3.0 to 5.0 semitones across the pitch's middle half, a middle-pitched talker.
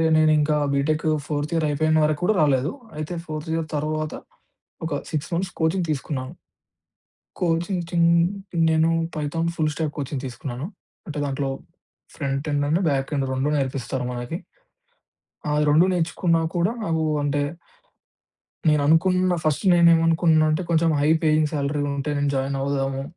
No: narrow, 2.6 semitones; medium, 155 Hz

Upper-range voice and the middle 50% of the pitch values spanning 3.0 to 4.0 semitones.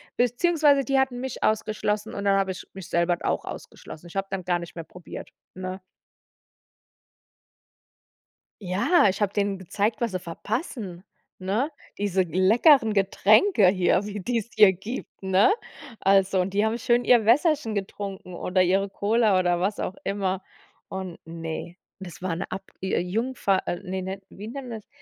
Yes: high, 195 Hz; average, 3.3 semitones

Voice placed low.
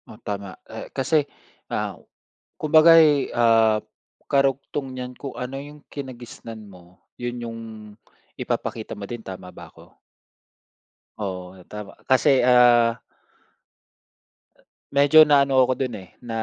Yes: low, 125 Hz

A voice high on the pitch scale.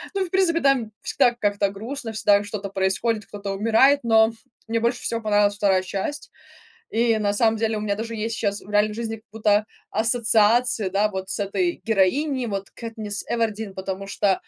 Yes: high, 220 Hz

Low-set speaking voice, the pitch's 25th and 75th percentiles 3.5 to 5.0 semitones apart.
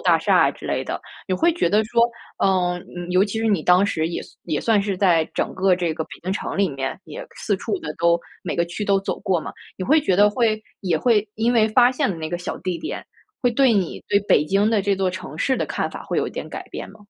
No: high, 195 Hz; average, 3.8 semitones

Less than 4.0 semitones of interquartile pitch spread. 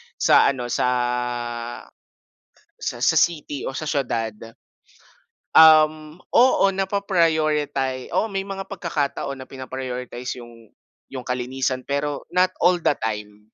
No: average, 4.7 semitones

